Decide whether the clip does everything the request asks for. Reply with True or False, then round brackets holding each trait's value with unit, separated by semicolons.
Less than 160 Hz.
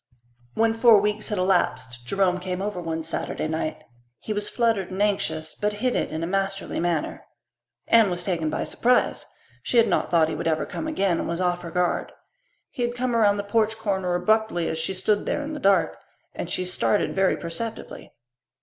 False (195 Hz)